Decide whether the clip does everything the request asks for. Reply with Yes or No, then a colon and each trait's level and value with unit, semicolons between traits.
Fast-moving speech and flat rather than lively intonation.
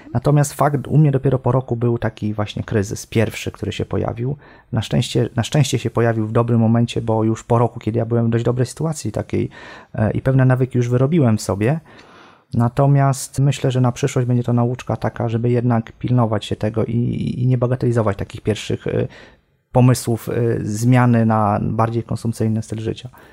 Yes: fast, 180 wpm; narrow, 2.3 semitones